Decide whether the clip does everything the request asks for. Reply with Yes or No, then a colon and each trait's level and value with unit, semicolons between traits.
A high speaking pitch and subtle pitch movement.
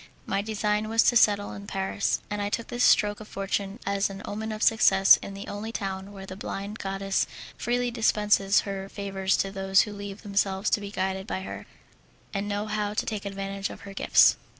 Yes: high, 200 Hz; narrow, 1.3 semitones